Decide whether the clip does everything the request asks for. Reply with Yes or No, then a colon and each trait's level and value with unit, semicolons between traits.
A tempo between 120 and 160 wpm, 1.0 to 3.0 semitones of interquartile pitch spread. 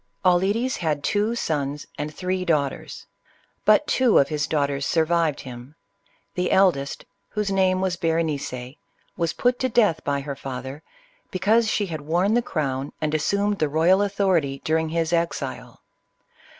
No: average, 150 wpm; average, 5.0 semitones